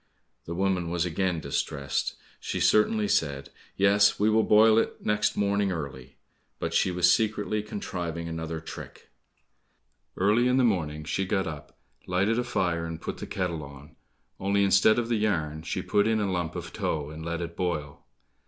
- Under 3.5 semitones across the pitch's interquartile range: No, average, 4.5 semitones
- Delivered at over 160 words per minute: Yes, average, 175 wpm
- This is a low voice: Yes, very low, 90 Hz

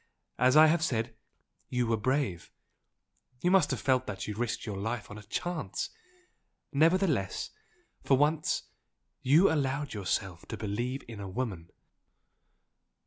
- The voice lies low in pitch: Yes, low, 125 Hz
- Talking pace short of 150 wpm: Yes, average, 140 wpm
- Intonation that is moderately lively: No, wide, 6.0 semitones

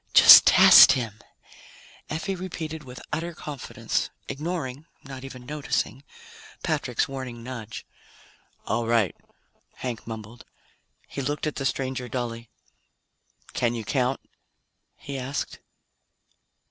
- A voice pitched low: Yes, low, 130 Hz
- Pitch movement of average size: Yes, average, 3.8 semitones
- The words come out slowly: Yes, slow, 110 wpm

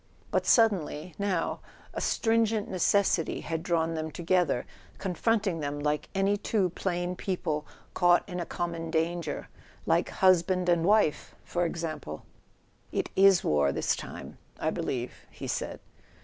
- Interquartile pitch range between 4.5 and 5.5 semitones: No, average, 3.0 semitones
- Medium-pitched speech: Yes, medium, 175 Hz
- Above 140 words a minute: No, slow, 135 wpm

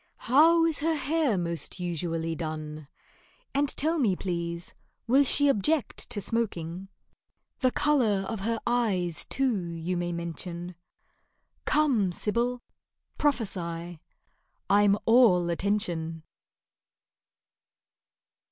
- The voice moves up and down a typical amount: No, wide, 6.8 semitones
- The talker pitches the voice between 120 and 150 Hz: No, high, 200 Hz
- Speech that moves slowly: Yes, slow, 95 wpm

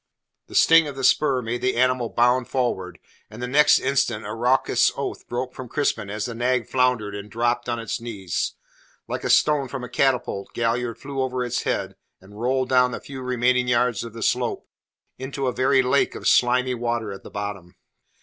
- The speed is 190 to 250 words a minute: Yes, average, 195 wpm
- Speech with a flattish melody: Yes, narrow, 1.9 semitones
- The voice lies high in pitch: No, low, 125 Hz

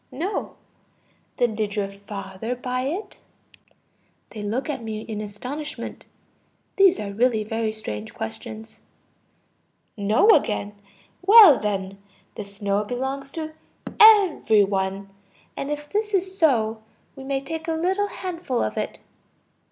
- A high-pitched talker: Yes, high, 235 Hz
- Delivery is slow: Yes, slow, 130 wpm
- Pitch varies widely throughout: Yes, wide, 7.2 semitones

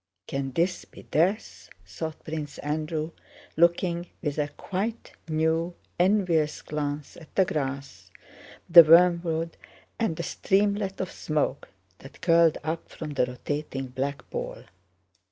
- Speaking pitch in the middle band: Yes, medium, 160 Hz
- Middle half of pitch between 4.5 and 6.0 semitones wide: No, average, 3.1 semitones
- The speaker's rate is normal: No, slow, 125 wpm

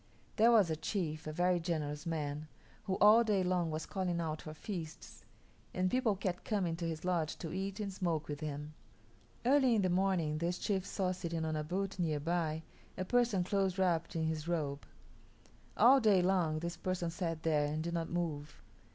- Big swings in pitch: No, average, 3.3 semitones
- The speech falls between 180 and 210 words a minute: Yes, average, 195 wpm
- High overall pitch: No, medium, 175 Hz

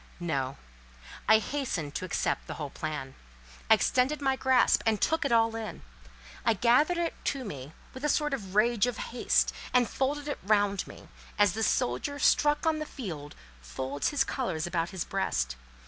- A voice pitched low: No, high, 220 Hz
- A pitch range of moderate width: No, wide, 8.4 semitones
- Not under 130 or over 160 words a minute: No, average, 180 wpm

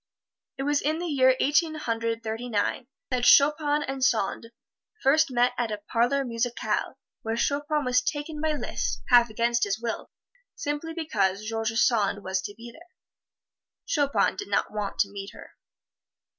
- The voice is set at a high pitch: Yes, high, 245 Hz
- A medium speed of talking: Yes, average, 160 wpm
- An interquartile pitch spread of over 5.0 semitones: No, average, 4.6 semitones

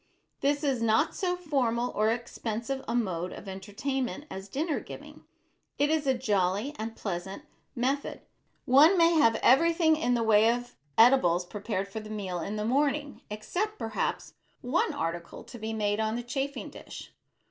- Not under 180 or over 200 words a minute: No, average, 165 wpm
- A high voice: Yes, high, 235 Hz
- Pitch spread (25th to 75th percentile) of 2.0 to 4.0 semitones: No, average, 5.1 semitones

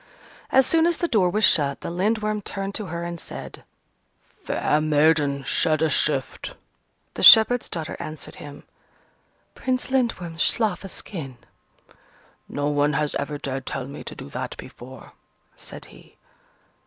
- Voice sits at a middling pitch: Yes, medium, 165 Hz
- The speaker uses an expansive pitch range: Yes, wide, 6.6 semitones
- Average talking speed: Yes, average, 150 wpm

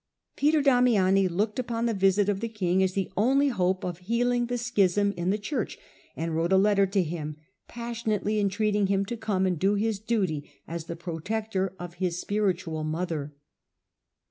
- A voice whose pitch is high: Yes, high, 195 Hz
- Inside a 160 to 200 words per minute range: Yes, average, 180 wpm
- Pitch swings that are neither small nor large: Yes, average, 3.7 semitones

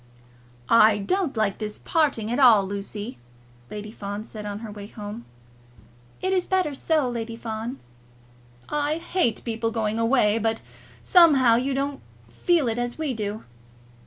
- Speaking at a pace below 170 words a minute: Yes, average, 150 wpm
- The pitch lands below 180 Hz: No, high, 230 Hz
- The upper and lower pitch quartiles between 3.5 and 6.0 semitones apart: Yes, average, 4.7 semitones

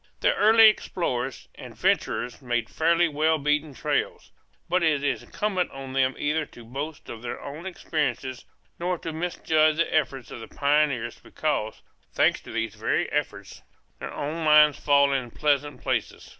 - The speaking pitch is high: No, medium, 145 Hz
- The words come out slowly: No, average, 160 wpm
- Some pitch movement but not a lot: Yes, average, 3.4 semitones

